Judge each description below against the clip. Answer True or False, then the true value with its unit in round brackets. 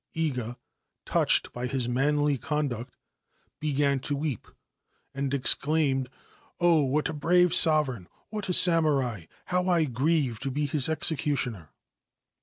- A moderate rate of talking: False (130 wpm)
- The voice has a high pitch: False (145 Hz)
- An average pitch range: True (3.7 semitones)